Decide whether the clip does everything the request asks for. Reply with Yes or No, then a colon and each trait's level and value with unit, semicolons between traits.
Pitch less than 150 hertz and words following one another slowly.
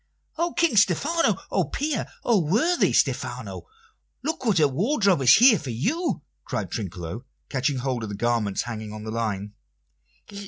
No: medium, 140 Hz; average, 155 wpm